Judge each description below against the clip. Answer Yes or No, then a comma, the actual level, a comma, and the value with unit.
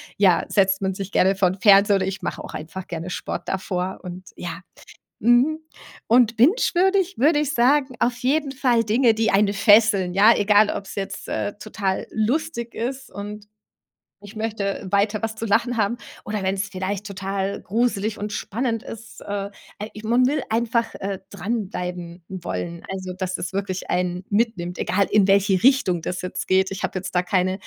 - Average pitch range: Yes, average, 3.5 semitones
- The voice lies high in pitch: Yes, high, 205 Hz